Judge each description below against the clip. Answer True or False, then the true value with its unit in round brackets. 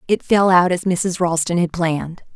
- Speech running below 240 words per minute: True (205 wpm)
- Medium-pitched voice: True (175 Hz)